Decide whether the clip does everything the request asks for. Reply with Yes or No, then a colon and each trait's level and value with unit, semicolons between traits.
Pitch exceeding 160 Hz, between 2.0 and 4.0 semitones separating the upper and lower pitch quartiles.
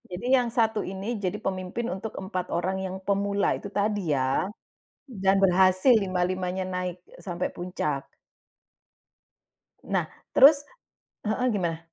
Yes: high, 190 Hz; narrow, 2.5 semitones